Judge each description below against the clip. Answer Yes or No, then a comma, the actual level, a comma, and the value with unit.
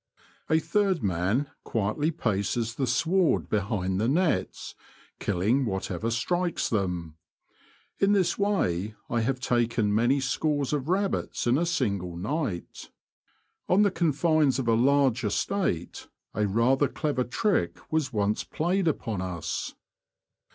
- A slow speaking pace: Yes, slow, 130 wpm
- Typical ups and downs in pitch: No, wide, 7.4 semitones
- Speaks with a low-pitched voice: Yes, low, 125 Hz